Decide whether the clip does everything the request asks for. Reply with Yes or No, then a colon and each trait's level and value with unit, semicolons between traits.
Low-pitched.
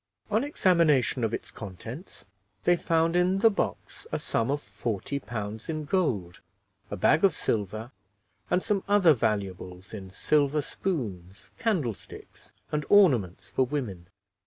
Yes: low, 130 Hz